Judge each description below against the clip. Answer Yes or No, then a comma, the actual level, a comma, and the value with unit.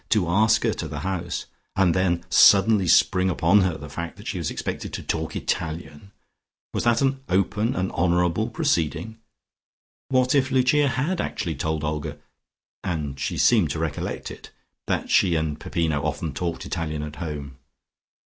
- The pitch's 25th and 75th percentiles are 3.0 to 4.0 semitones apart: No, average, 5.2 semitones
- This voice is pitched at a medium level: No, very low, 85 Hz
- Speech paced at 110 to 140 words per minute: No, average, 165 wpm